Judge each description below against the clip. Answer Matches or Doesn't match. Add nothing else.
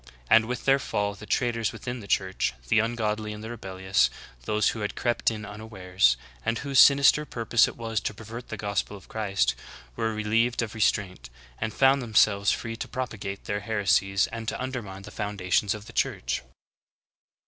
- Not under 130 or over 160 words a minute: Doesn't match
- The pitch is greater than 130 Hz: Doesn't match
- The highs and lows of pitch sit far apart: Doesn't match